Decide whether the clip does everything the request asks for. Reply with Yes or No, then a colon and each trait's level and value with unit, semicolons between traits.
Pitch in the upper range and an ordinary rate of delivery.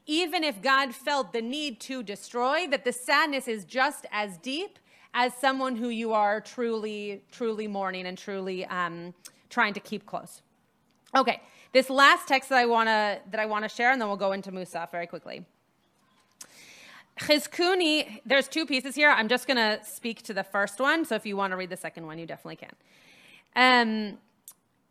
Yes: high, 230 Hz; average, 180 wpm